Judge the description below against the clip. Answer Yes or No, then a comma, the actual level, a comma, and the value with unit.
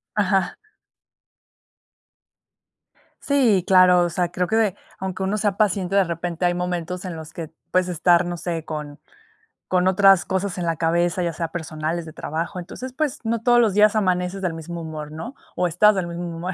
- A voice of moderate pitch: Yes, medium, 180 Hz